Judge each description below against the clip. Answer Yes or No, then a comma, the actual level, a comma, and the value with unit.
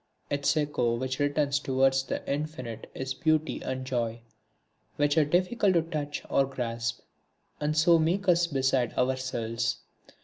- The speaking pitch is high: No, medium, 140 Hz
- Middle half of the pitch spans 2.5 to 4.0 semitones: Yes, average, 3.5 semitones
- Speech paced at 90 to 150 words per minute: Yes, average, 140 wpm